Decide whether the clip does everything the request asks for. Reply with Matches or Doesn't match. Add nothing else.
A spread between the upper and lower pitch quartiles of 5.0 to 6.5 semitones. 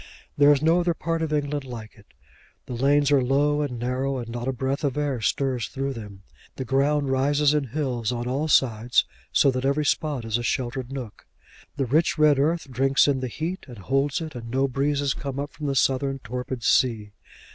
Doesn't match